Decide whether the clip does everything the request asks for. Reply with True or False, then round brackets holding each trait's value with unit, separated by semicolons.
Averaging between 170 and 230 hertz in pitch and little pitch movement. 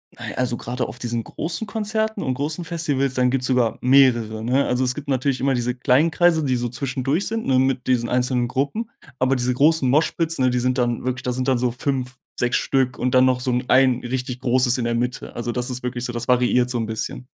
False (125 Hz; 1.8 semitones)